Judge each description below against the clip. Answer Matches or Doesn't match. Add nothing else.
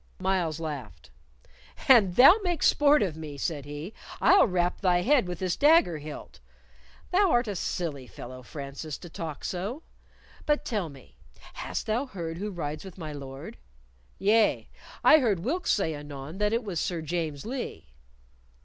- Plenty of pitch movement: Matches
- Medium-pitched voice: Matches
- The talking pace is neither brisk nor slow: Matches